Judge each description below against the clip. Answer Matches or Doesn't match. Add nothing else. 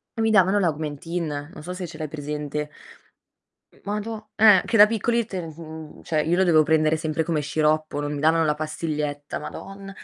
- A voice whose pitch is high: Doesn't match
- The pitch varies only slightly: Doesn't match